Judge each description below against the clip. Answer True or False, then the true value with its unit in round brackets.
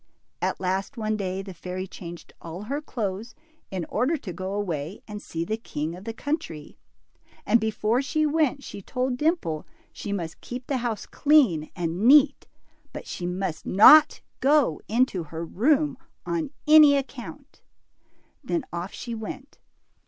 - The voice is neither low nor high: False (215 Hz)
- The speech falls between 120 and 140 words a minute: False (155 wpm)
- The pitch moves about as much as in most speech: False (7.1 semitones)